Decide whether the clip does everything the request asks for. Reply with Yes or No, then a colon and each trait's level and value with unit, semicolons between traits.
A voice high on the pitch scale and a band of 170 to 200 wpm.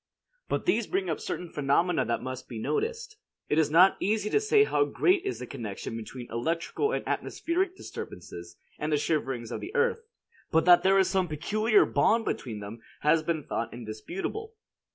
No: medium, 170 Hz; average, 180 wpm